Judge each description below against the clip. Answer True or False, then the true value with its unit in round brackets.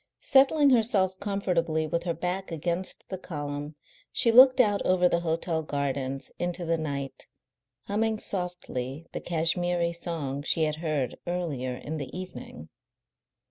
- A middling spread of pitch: True (3.7 semitones)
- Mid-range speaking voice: True (170 Hz)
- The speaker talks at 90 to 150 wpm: True (140 wpm)